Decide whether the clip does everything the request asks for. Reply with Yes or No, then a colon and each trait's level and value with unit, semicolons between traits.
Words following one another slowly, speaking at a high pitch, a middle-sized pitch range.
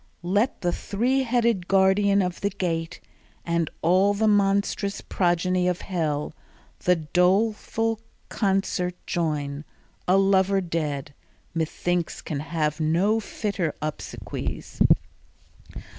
No: slow, 105 wpm; medium, 180 Hz; average, 3.4 semitones